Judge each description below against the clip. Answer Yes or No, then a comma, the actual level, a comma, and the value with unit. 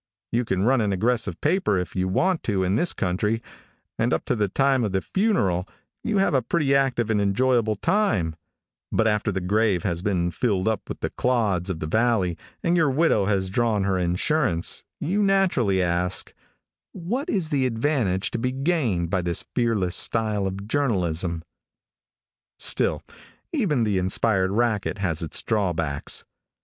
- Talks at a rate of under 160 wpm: No, average, 165 wpm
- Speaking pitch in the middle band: No, low, 105 Hz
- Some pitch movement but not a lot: No, wide, 6.0 semitones